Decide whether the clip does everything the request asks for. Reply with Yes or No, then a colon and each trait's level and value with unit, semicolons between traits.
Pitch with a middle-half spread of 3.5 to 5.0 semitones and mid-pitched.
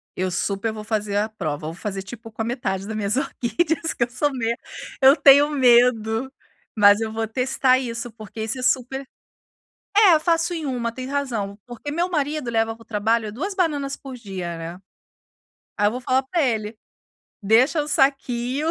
No: average, 4.2 semitones; high, 240 Hz